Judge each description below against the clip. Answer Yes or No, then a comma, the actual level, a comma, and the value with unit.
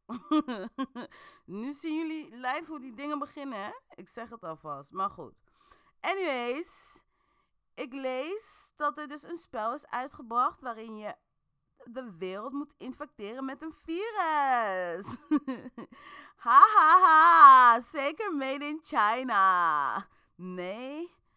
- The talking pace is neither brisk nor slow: No, slow, 120 wpm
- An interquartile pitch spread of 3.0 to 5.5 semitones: Yes, average, 5.0 semitones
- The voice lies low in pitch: No, very high, 280 Hz